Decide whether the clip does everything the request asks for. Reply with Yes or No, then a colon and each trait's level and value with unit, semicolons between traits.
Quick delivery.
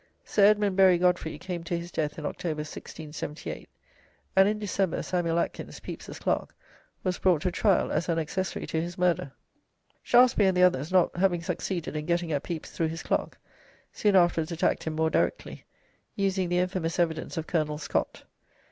No: average, 175 wpm